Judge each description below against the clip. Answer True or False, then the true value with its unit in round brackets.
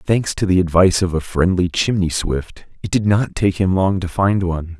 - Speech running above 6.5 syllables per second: False (5.1 syllables/s)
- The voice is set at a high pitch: False (90 Hz)